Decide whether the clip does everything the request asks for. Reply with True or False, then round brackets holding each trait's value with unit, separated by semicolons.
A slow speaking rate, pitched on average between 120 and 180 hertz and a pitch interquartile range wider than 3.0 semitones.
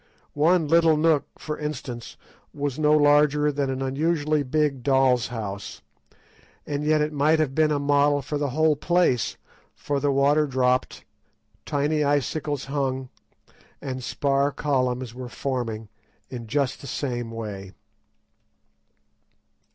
False (130 wpm; 140 Hz; 2.7 semitones)